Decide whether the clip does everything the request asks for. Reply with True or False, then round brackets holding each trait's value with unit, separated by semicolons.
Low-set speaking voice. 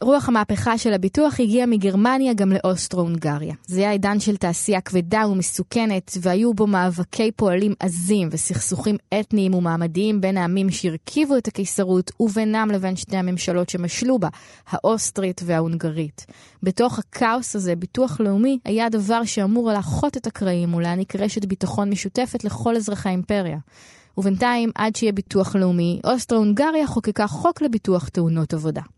False (200 Hz)